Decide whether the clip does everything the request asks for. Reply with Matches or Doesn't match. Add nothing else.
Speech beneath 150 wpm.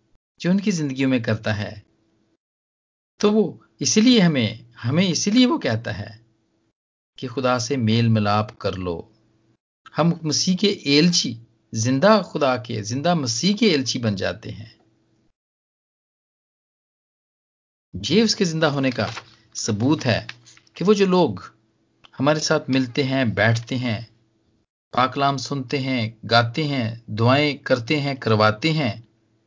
Matches